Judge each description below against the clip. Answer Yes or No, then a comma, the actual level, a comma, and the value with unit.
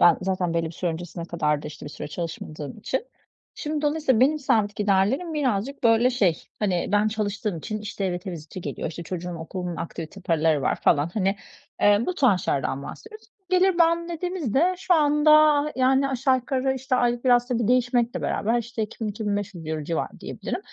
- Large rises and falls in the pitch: Yes, wide, 7.3 semitones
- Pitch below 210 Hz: No, high, 215 Hz